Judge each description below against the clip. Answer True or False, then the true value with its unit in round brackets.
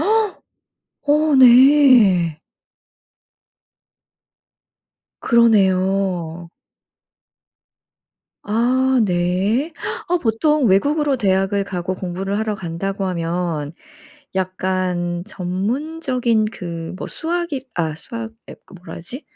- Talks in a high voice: True (195 Hz)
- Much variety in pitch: True (6.2 semitones)